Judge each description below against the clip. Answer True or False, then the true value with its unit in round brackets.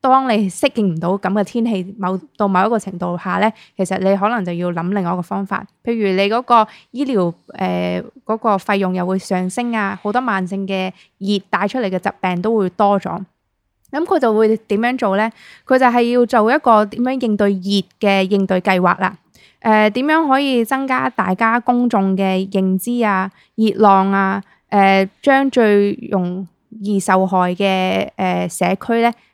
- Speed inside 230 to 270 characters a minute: True (260 characters per minute)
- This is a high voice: True (200 Hz)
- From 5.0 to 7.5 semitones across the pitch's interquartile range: False (3.3 semitones)